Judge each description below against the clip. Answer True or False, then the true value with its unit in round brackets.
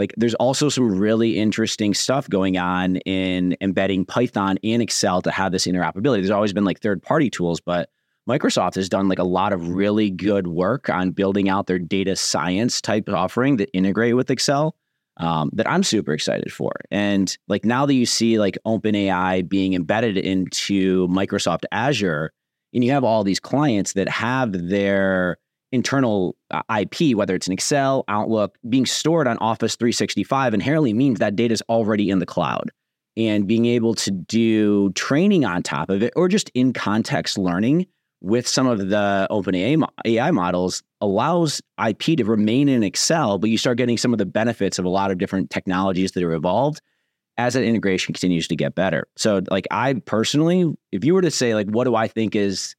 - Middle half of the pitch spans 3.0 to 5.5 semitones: True (3.9 semitones)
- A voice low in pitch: True (100 Hz)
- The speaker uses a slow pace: False (190 wpm)